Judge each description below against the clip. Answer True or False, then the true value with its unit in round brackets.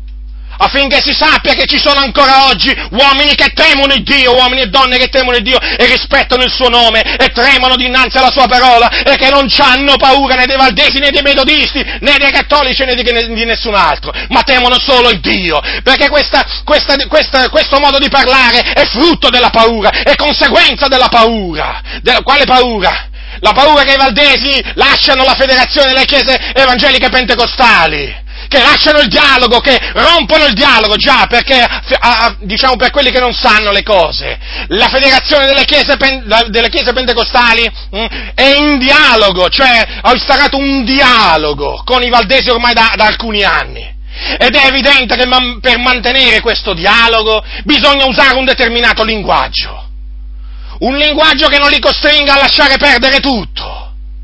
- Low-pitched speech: False (260 Hz)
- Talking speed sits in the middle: False (175 wpm)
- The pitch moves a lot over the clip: False (2.8 semitones)